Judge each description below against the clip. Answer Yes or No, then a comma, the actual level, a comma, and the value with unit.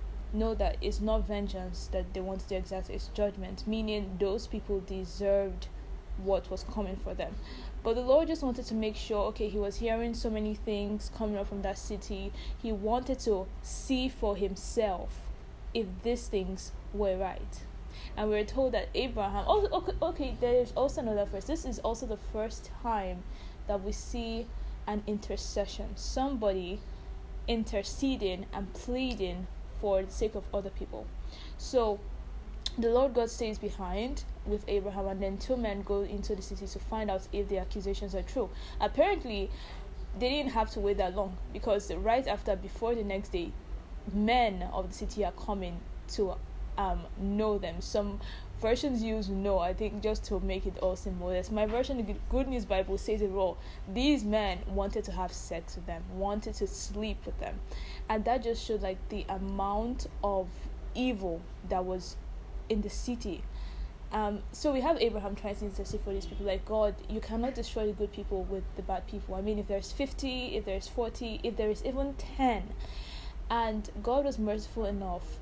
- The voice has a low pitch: No, high, 210 Hz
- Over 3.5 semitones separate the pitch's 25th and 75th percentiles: No, average, 2.7 semitones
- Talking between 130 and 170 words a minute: No, average, 180 wpm